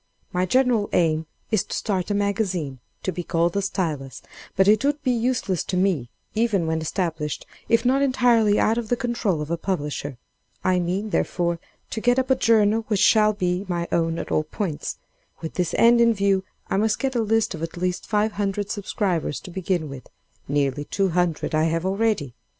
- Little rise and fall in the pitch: No, average, 4.8 semitones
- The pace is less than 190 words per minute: No, average, 195 wpm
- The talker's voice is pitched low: No, high, 190 Hz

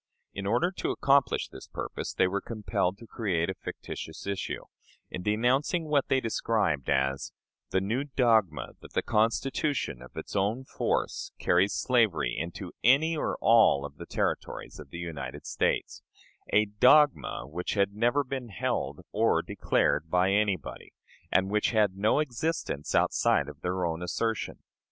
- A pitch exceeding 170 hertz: No, low, 105 Hz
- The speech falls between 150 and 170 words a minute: Yes, average, 155 wpm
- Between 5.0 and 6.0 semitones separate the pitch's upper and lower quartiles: Yes, wide, 5.5 semitones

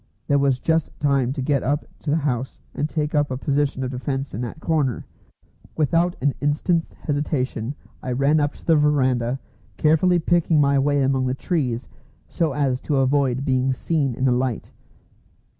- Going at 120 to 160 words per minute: No, average, 175 wpm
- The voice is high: No, medium, 140 Hz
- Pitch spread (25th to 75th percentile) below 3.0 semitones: Yes, narrow, 2.5 semitones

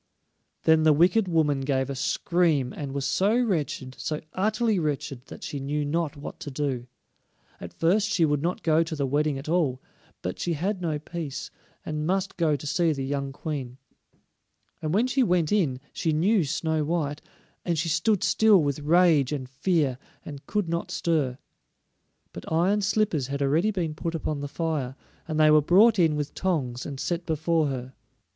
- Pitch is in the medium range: Yes, medium, 155 Hz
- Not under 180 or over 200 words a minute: Yes, average, 185 wpm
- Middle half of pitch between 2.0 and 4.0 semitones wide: Yes, average, 3.7 semitones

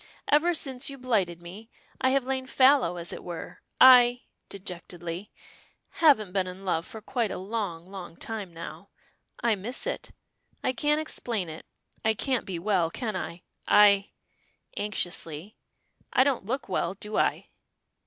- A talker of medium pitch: No, high, 210 Hz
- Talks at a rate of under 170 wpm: Yes, average, 155 wpm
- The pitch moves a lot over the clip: Yes, wide, 6.0 semitones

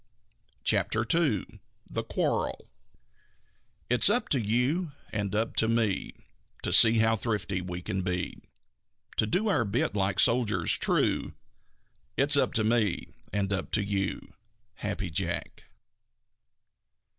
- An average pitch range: Yes, average, 3.8 semitones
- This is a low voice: Yes, low, 110 Hz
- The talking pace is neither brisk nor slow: No, slow, 125 wpm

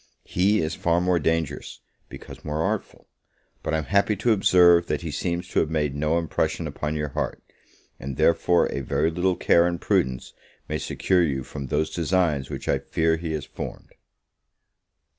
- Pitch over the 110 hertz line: No, very low, 80 Hz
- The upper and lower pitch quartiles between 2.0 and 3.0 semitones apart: Yes, narrow, 2.5 semitones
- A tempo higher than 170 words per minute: Yes, average, 180 wpm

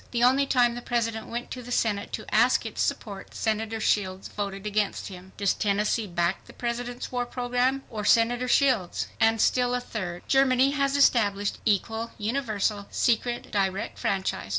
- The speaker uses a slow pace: No, average, 165 wpm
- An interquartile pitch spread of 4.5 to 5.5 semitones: No, average, 3.3 semitones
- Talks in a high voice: Yes, high, 225 Hz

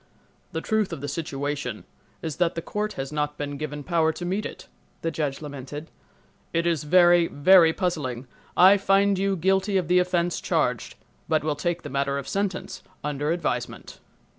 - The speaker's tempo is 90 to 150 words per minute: No, average, 170 wpm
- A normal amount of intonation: Yes, average, 3.8 semitones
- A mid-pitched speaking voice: Yes, medium, 165 Hz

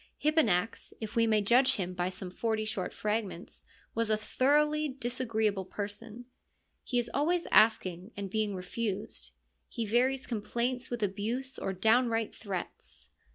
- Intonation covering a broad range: No, average, 3.5 semitones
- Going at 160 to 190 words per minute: No, average, 140 wpm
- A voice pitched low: No, high, 220 Hz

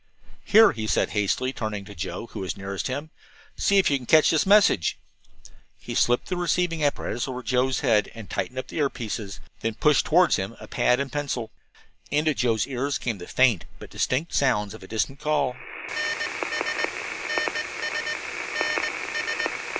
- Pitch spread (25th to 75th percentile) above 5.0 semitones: Yes, wide, 5.4 semitones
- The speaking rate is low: No, average, 160 wpm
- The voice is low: Yes, low, 125 Hz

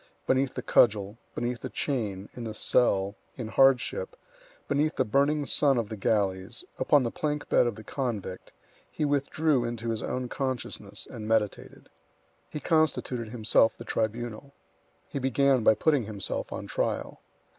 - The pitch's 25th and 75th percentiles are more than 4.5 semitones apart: No, average, 4.1 semitones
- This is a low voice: Yes, low, 120 Hz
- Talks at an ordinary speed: Yes, average, 155 wpm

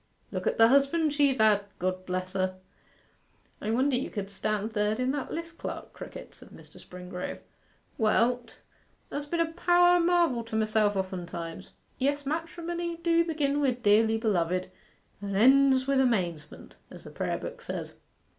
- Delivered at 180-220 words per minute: No, average, 165 wpm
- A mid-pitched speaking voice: No, high, 240 Hz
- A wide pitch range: Yes, wide, 6.4 semitones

